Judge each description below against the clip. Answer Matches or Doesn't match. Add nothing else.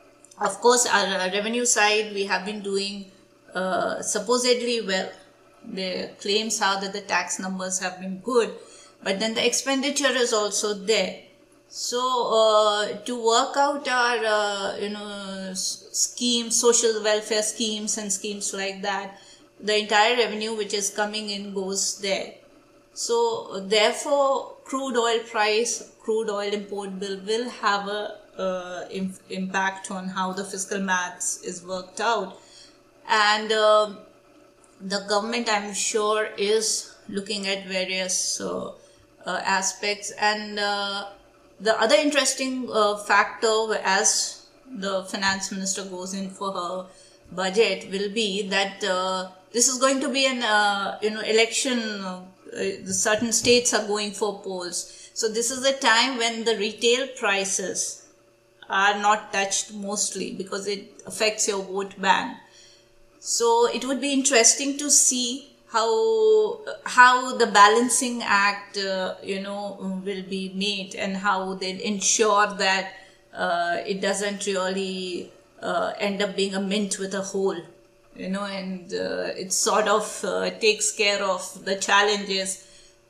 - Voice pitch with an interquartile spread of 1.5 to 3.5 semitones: Matches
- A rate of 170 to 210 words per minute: Doesn't match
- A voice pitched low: Doesn't match